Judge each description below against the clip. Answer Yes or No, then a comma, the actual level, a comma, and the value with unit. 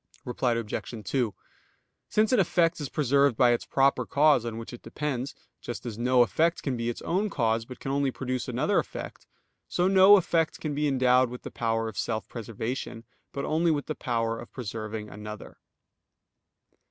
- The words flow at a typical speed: Yes, average, 180 wpm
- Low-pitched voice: Yes, low, 125 Hz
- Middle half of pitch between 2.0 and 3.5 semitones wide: No, average, 4.5 semitones